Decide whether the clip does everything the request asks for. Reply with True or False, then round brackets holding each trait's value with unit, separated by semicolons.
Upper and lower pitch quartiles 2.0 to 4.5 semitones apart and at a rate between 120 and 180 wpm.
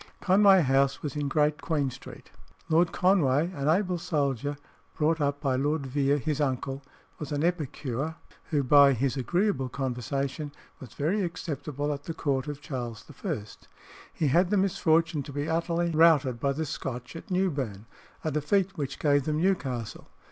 True (3.4 semitones; 160 wpm)